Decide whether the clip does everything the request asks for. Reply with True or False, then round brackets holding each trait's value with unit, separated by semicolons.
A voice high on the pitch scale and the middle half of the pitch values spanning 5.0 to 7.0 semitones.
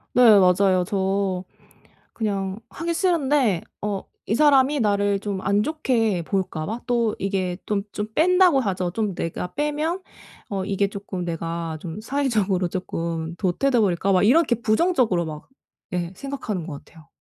True (200 Hz; 5.5 semitones)